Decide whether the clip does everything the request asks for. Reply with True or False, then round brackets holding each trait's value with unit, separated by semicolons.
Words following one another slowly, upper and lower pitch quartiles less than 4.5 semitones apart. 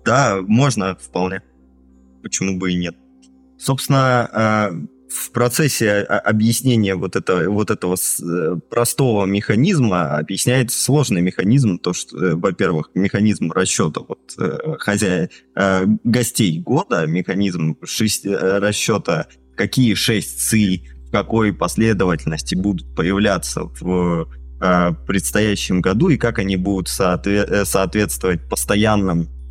True (100 wpm; 3.9 semitones)